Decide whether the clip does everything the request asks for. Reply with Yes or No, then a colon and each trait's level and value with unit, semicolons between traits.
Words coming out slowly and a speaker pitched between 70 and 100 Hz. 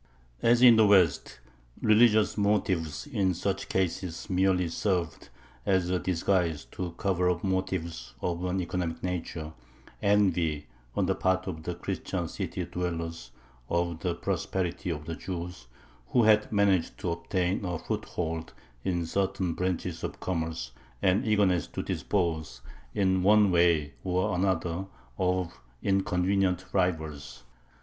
Yes: slow, 130 wpm; very low, 90 Hz